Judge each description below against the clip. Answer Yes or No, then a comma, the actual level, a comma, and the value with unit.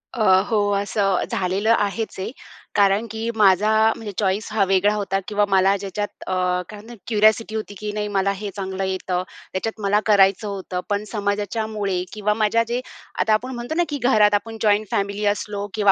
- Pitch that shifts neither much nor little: No, narrow, 1.8 semitones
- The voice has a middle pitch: No, high, 205 Hz